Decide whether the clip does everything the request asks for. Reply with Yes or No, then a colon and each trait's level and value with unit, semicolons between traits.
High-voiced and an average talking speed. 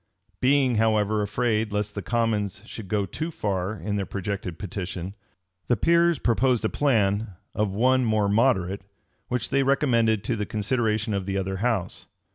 No: low, 110 Hz; average, 165 wpm